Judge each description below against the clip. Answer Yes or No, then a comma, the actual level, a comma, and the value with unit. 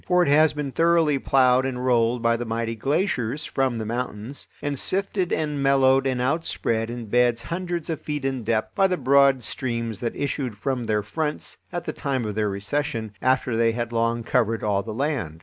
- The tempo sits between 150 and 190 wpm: No, average, 200 wpm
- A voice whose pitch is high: No, low, 125 Hz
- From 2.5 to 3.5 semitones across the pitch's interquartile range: No, average, 4.1 semitones